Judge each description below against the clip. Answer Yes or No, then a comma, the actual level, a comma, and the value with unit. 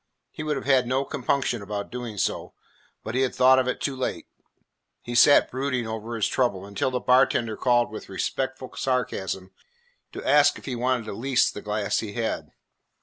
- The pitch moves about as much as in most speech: Yes, average, 3.2 semitones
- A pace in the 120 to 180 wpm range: No, average, 190 wpm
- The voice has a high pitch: No, low, 125 Hz